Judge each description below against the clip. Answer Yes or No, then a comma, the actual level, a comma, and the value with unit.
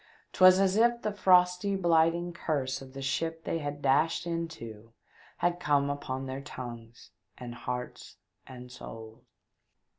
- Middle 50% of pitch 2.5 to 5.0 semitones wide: No, wide, 5.5 semitones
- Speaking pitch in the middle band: Yes, medium, 145 Hz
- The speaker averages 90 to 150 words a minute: Yes, average, 140 wpm